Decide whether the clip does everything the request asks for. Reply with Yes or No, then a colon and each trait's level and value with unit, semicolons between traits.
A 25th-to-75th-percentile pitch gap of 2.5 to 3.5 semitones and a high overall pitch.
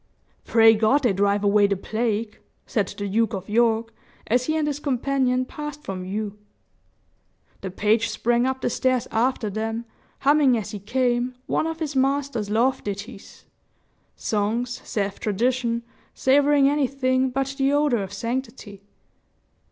No: average, 4.0 semitones; high, 235 Hz